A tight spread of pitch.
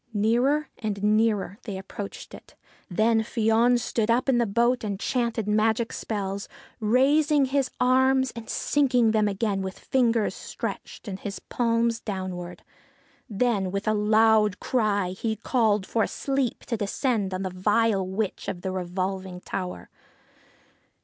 No: average, 3.3 semitones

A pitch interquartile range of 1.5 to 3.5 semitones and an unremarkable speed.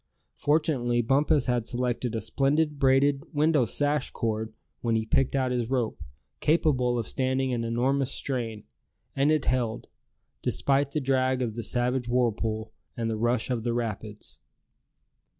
Yes: average, 2.9 semitones; average, 150 wpm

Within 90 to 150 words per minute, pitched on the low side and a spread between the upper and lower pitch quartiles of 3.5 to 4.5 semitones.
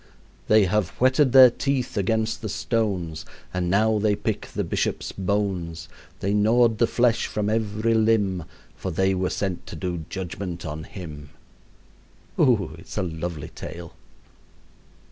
Yes: average, 145 wpm; low, 100 Hz; average, 4.0 semitones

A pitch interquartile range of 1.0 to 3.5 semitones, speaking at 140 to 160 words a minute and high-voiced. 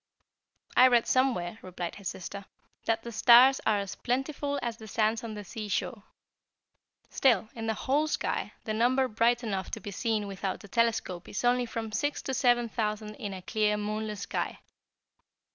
No: average, 2.8 semitones; average, 175 wpm; high, 220 Hz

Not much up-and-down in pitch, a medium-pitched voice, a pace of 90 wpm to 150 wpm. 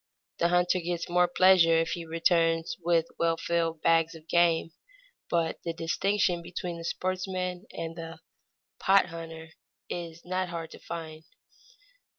Yes: narrow, 1.4 semitones; medium, 170 Hz; average, 145 wpm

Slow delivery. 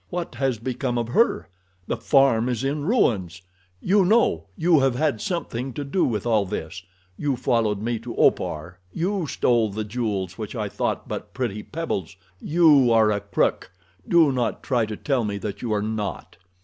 No: average, 180 wpm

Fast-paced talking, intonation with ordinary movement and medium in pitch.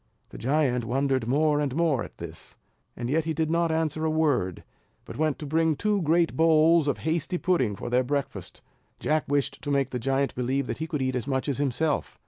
Yes: fast, 210 wpm; average, 3.4 semitones; medium, 145 Hz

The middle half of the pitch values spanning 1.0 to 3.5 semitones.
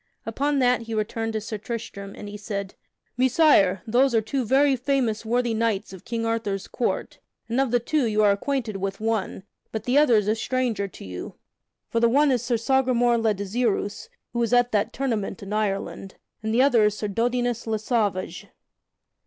Yes: average, 2.9 semitones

